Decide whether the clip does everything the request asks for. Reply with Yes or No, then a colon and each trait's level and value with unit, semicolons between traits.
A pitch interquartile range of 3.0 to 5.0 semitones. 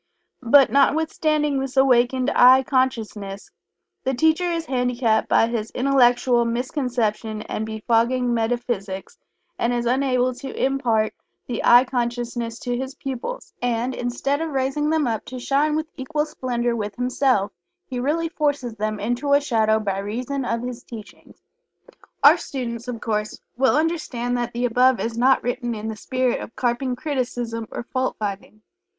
No: narrow, 2.5 semitones